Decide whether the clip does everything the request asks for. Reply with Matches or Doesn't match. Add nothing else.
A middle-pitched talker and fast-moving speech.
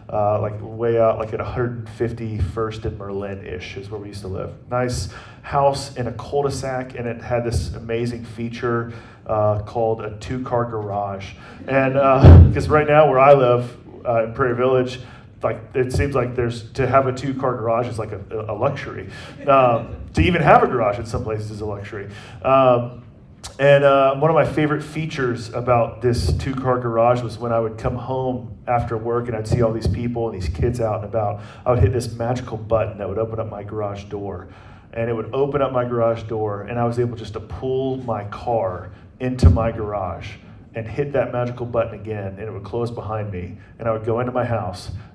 Doesn't match